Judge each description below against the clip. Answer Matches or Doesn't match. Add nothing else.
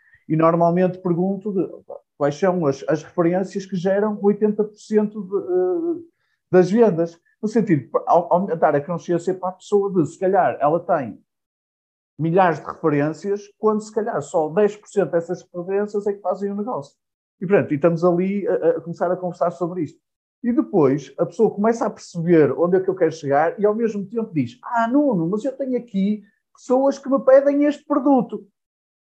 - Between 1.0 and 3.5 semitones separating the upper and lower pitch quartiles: Doesn't match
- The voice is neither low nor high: Doesn't match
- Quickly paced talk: Doesn't match